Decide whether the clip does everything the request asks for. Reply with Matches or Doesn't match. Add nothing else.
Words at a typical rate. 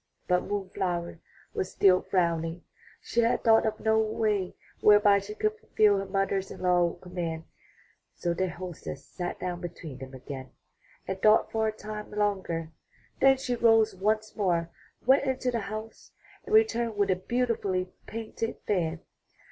Matches